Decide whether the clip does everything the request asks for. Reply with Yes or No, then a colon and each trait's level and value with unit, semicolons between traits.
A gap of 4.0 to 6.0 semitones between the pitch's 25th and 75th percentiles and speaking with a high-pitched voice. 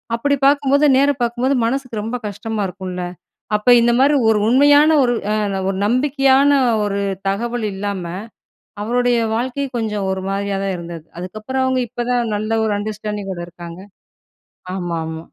Yes: average, 4.8 semitones; high, 225 Hz